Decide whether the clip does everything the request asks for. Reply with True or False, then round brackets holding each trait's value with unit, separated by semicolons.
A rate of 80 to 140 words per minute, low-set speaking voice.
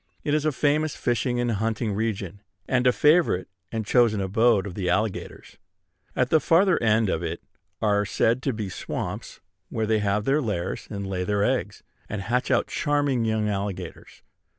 False (175 wpm; 110 Hz)